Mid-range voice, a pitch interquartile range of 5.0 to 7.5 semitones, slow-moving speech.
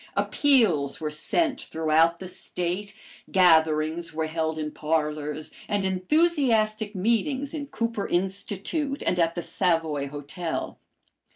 Yes: medium, 180 Hz; wide, 5.6 semitones; slow, 115 wpm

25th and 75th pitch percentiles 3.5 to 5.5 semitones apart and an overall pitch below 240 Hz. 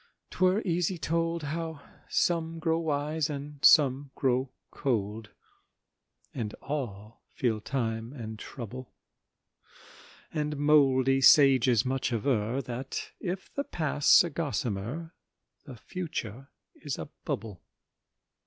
Yes: average, 5.1 semitones; medium, 140 Hz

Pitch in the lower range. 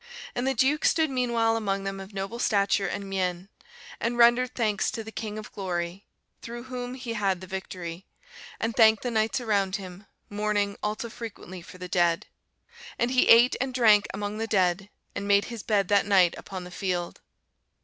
No: high, 205 Hz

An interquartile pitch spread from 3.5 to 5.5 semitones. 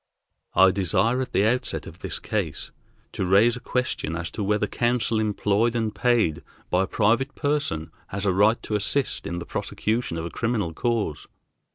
Yes: average, 4.0 semitones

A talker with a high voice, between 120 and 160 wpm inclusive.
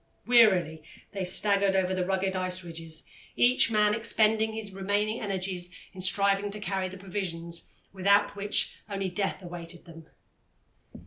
Yes: high, 195 Hz; average, 140 wpm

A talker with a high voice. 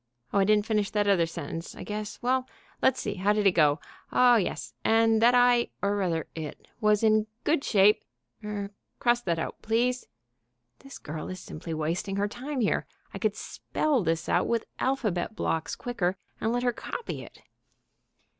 Yes: high, 210 Hz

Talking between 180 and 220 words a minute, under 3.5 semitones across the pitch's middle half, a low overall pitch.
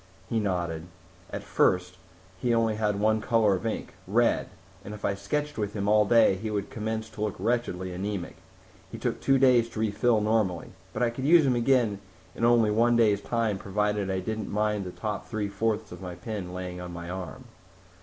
Yes: average, 200 wpm; average, 3.0 semitones; low, 105 Hz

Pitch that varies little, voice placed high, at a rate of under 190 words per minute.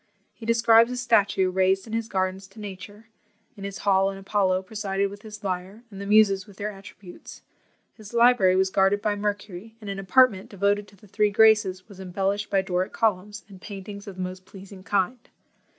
No: narrow, 1.8 semitones; high, 200 Hz; average, 195 wpm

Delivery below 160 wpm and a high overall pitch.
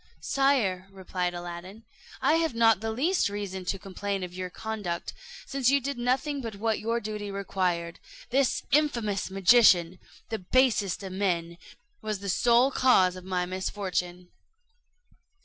Yes: average, 145 wpm; high, 200 Hz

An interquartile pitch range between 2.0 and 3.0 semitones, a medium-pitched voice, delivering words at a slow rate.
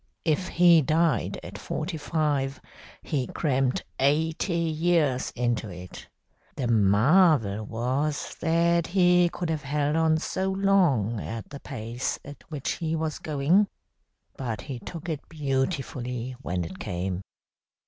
No: average, 5.1 semitones; medium, 145 Hz; slow, 130 wpm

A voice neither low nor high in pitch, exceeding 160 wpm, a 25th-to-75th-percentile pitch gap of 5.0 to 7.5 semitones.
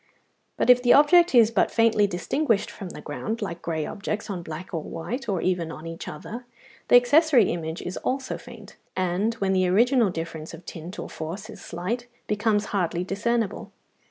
No: high, 200 Hz; average, 185 wpm; average, 5.3 semitones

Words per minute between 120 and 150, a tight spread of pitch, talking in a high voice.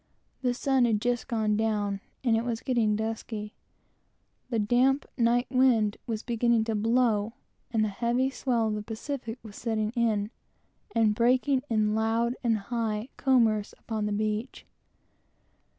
Yes: average, 145 wpm; narrow, 2.2 semitones; high, 225 Hz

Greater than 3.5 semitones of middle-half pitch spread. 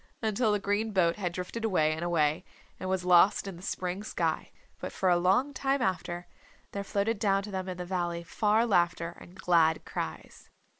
No: average, 3.0 semitones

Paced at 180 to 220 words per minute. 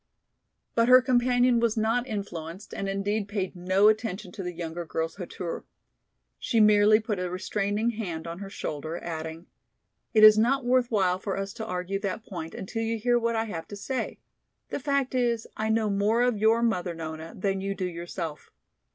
Yes: average, 185 wpm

